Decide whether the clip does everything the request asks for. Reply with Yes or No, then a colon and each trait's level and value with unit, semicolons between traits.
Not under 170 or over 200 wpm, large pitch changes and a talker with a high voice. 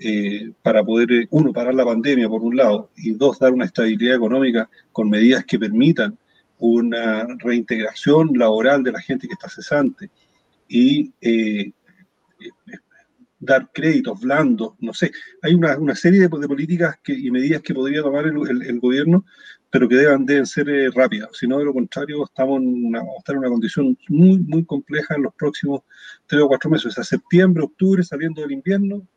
No: fast, 190 wpm; wide, 6.1 semitones; medium, 140 Hz